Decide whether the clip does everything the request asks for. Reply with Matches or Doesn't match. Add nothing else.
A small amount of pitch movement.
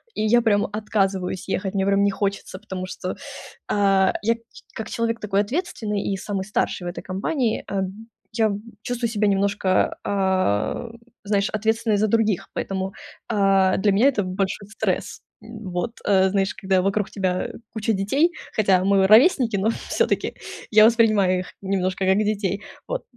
Matches